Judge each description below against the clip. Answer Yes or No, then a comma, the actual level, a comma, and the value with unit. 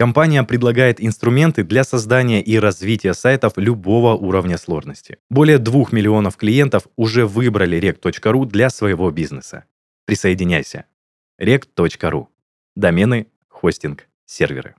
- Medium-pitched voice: No, low, 110 Hz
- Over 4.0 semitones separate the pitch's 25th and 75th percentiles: Yes, average, 4.6 semitones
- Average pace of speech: No, slow, 105 wpm